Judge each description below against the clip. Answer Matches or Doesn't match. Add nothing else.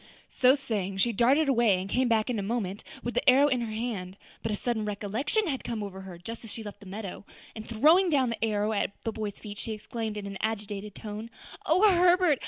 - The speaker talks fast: Matches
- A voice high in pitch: Matches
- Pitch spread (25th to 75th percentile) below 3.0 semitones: Doesn't match